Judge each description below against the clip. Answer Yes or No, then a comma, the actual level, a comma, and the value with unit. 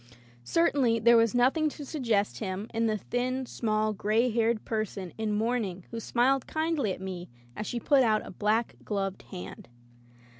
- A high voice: Yes, high, 225 Hz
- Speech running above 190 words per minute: No, average, 165 wpm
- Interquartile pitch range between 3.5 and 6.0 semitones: No, average, 2.9 semitones